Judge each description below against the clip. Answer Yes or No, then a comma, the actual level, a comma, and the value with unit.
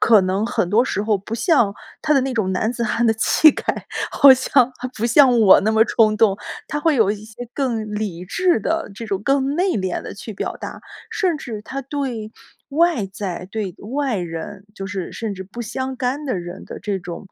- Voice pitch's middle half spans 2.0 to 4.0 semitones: No, average, 4.9 semitones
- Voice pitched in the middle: No, high, 225 Hz